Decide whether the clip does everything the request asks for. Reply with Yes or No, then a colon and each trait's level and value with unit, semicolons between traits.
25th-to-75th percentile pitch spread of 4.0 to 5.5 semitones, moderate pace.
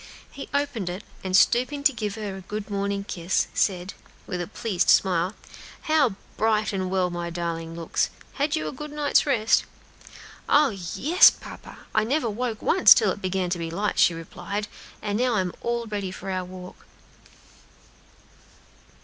Yes: average, 4.5 semitones; average, 165 wpm